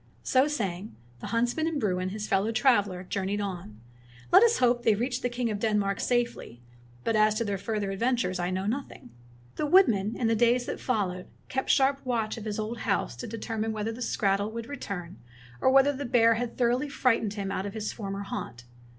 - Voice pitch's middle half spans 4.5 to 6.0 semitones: No, average, 3.7 semitones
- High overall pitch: Yes, high, 220 Hz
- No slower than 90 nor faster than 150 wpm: No, fast, 205 wpm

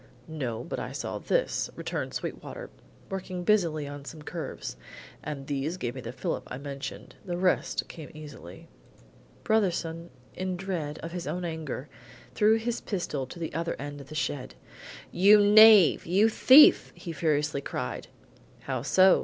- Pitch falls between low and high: Yes, medium, 165 Hz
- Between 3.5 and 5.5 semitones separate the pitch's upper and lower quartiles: Yes, average, 4.8 semitones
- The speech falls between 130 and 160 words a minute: Yes, average, 155 wpm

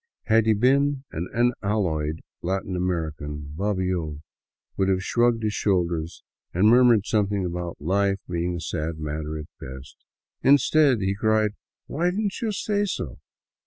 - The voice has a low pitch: Yes, very low, 95 Hz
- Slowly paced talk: No, average, 150 wpm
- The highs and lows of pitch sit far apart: Yes, wide, 5.9 semitones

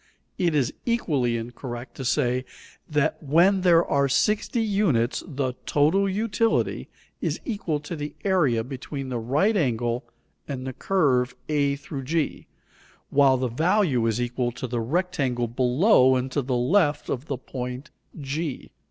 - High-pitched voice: No, medium, 140 Hz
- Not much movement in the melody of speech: No, average, 5.3 semitones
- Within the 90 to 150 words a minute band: Yes, average, 145 wpm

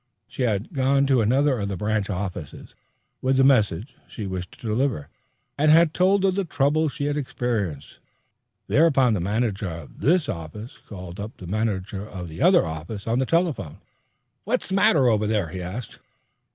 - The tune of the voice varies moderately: No, wide, 6.6 semitones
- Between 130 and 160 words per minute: No, average, 170 wpm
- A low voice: Yes, low, 110 Hz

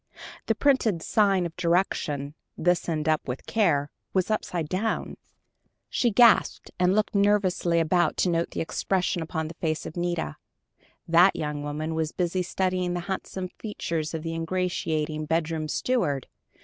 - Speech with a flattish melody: No, average, 3.0 semitones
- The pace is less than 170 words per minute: Yes, average, 150 wpm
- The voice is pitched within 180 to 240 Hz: No, medium, 170 Hz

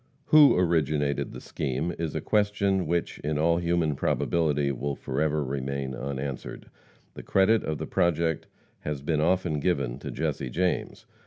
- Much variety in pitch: No, average, 3.7 semitones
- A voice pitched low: Yes, very low, 75 Hz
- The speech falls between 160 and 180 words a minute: No, average, 150 wpm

